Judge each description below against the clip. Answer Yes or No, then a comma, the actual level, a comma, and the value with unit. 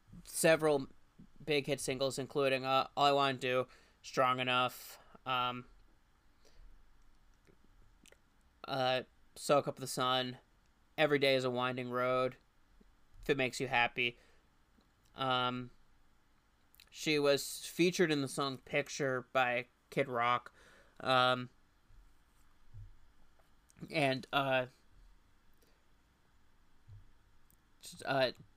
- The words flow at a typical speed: No, slow, 95 wpm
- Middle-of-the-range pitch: No, low, 130 Hz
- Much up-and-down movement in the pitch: No, narrow, 2.5 semitones